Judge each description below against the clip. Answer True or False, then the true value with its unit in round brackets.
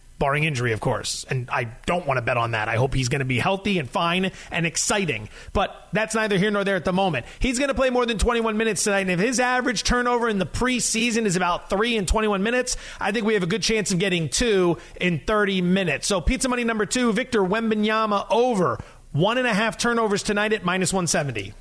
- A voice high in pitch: True (200 Hz)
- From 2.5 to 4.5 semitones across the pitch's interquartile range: False (5.1 semitones)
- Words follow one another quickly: True (235 wpm)